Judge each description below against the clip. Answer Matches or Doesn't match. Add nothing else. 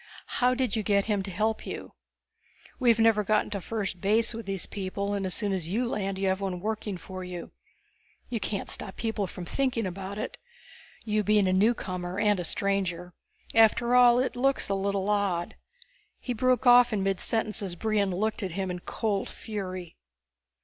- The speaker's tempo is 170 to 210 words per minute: Matches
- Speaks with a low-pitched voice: Doesn't match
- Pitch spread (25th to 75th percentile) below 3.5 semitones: Matches